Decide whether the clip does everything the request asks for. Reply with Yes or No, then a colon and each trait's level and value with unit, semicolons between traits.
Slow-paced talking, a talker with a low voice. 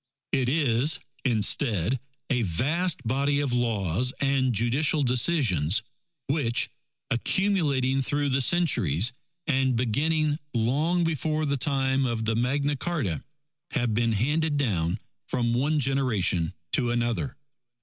Yes: slow, 120 wpm; low, 130 Hz